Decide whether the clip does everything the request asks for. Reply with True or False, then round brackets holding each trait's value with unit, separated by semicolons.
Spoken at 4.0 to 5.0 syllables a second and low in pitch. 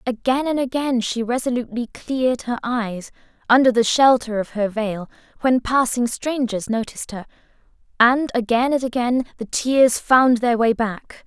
False (4.6 syllables/s; 240 Hz)